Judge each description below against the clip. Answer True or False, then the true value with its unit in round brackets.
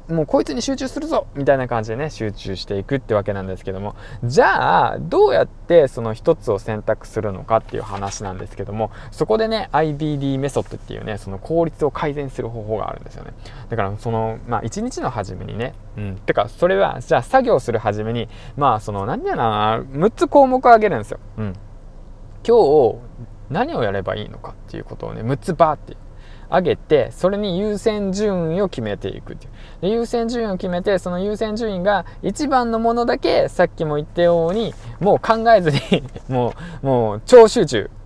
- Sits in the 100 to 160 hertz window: True (135 Hz)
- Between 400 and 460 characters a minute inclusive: False (380 characters per minute)